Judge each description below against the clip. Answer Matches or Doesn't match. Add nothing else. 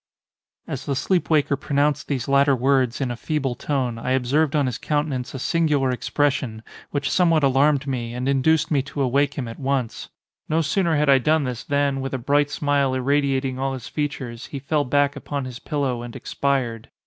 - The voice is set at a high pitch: Doesn't match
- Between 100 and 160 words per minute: Doesn't match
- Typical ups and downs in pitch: Doesn't match